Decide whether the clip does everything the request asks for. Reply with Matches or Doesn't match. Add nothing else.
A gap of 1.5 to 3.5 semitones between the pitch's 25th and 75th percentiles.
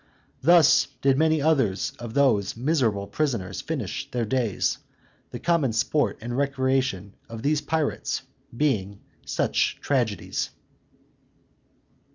Doesn't match